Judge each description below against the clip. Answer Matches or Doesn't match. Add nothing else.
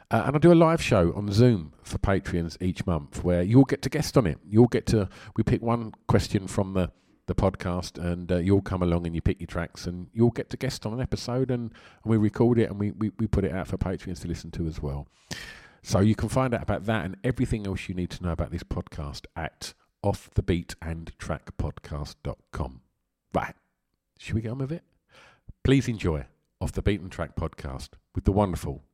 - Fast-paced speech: Matches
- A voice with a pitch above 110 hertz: Doesn't match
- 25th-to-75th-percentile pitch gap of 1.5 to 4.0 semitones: Doesn't match